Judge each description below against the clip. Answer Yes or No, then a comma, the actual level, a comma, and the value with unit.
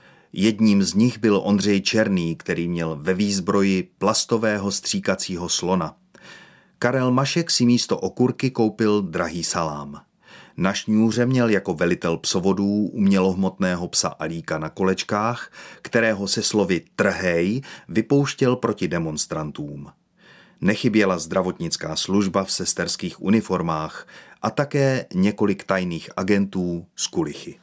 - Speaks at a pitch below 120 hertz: Yes, low, 100 Hz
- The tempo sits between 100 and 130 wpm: Yes, slow, 115 wpm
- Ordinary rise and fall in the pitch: Yes, average, 4.0 semitones